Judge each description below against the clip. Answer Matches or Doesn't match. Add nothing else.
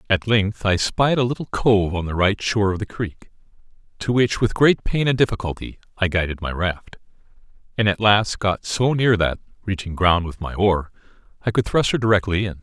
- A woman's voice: Doesn't match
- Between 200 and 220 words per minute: Matches